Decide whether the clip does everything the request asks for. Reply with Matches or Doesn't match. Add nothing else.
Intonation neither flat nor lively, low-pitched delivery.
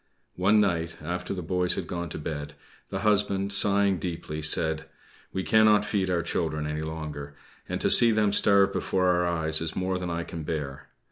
Matches